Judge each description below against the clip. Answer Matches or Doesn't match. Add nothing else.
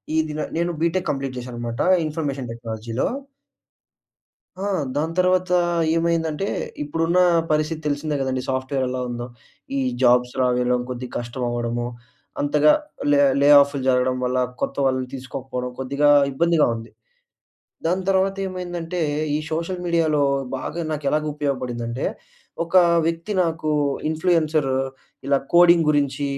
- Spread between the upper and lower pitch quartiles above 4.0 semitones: Matches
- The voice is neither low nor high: Matches